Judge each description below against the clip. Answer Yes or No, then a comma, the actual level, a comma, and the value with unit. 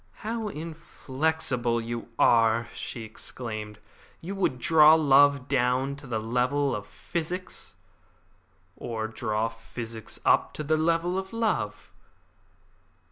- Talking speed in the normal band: No, slow, 115 wpm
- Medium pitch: No, low, 130 Hz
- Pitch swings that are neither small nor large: No, wide, 5.7 semitones